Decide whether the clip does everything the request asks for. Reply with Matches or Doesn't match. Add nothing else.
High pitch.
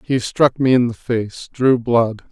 Doesn't match